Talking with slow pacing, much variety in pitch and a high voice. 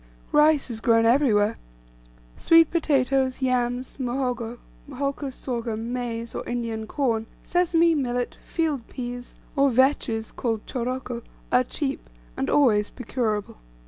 No: slow, 115 wpm; average, 3.1 semitones; very high, 250 Hz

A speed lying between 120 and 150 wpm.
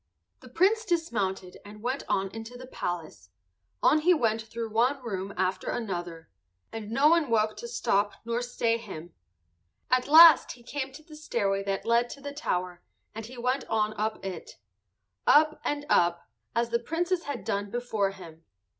No: average, 170 wpm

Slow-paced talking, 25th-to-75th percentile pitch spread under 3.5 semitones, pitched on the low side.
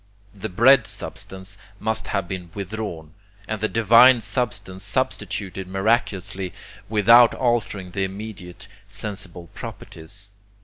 Yes: slow, 105 wpm; average, 2.8 semitones; low, 100 Hz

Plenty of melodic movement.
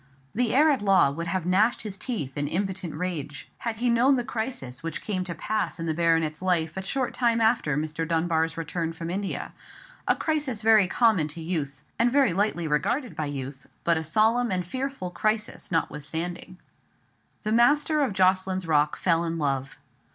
Yes: wide, 5.8 semitones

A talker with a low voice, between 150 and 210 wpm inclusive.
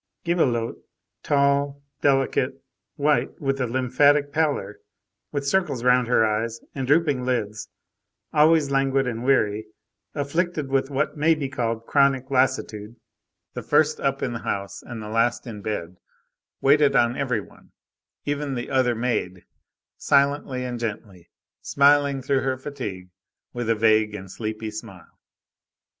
No: low, 130 Hz; average, 140 wpm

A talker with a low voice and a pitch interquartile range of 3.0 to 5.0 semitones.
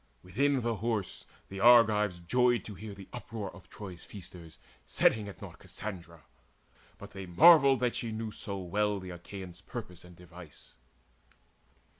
Yes: low, 100 Hz; average, 4.3 semitones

